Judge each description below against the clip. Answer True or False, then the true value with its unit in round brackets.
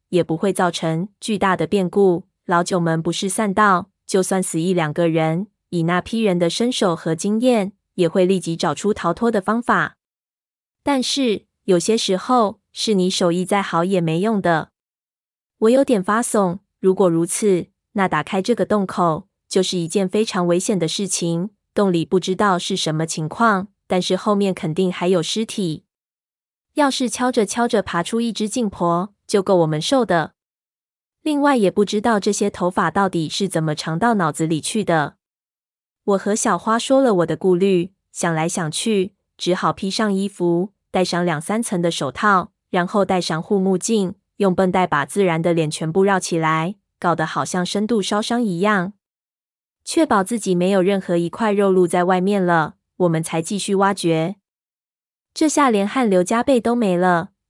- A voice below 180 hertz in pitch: False (190 Hz)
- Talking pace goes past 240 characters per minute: True (250 characters per minute)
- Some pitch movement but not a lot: True (3.5 semitones)